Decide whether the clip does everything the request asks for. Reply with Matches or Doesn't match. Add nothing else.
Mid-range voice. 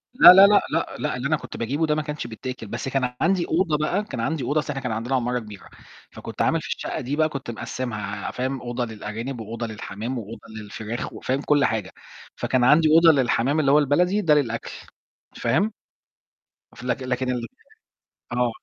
Doesn't match